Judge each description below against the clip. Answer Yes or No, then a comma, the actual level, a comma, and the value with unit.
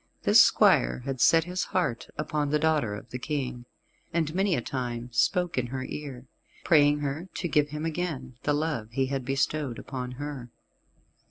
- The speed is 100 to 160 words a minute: No, average, 175 wpm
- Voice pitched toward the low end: No, medium, 145 Hz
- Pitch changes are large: No, average, 3.6 semitones